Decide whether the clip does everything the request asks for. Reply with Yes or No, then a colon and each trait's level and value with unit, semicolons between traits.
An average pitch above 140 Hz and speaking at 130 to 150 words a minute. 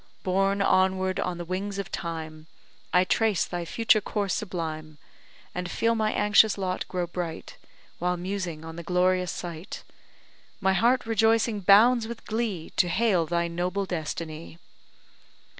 Yes: medium, 185 Hz; average, 140 wpm